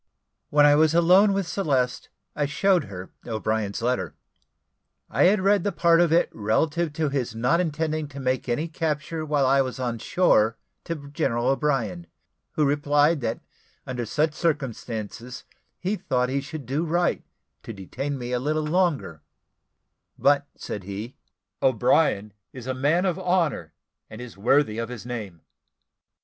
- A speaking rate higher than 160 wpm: No, average, 155 wpm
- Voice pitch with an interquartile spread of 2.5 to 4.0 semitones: No, average, 5.2 semitones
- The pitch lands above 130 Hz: Yes, medium, 140 Hz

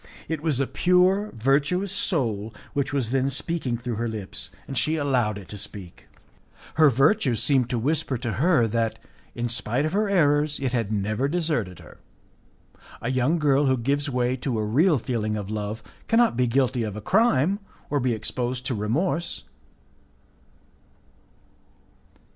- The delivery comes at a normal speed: Yes, average, 160 wpm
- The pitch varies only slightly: No, average, 5.0 semitones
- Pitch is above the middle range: No, low, 130 Hz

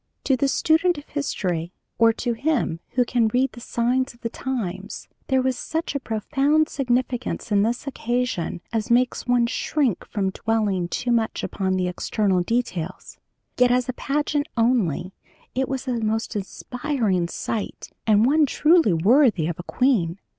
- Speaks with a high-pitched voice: Yes, high, 240 Hz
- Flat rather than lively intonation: No, average, 4.6 semitones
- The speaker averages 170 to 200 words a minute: No, average, 160 wpm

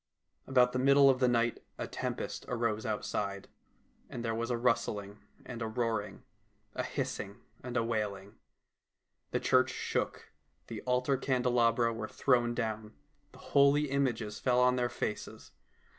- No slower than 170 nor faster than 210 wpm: No, average, 145 wpm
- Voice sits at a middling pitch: No, low, 120 Hz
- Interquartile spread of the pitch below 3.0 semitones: Yes, narrow, 2.4 semitones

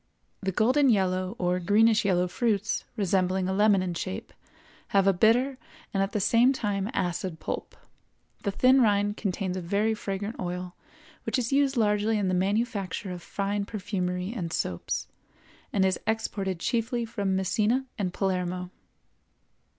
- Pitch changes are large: No, average, 3.2 semitones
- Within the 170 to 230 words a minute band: No, average, 150 wpm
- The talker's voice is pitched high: Yes, high, 200 Hz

